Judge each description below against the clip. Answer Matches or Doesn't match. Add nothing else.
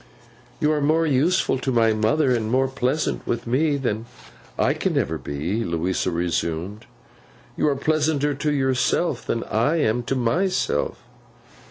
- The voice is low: Matches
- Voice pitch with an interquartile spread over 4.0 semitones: Matches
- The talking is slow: Doesn't match